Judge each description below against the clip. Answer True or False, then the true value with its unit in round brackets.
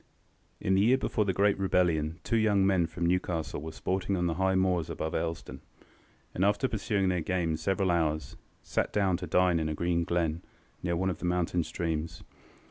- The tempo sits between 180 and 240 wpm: True (195 wpm)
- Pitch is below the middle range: True (90 Hz)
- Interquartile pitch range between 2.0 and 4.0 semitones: True (2.5 semitones)